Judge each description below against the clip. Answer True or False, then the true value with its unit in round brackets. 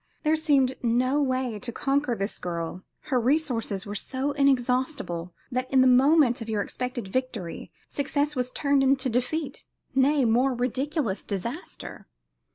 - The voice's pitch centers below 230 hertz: False (255 Hz)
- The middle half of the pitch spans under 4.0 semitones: True (3.1 semitones)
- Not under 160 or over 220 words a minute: False (145 wpm)